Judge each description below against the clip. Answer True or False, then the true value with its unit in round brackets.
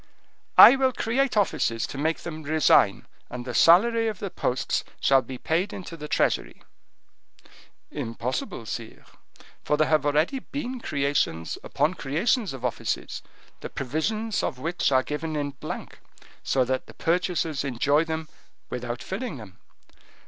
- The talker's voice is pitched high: False (155 Hz)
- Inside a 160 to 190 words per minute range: False (145 wpm)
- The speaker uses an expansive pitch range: True (6.0 semitones)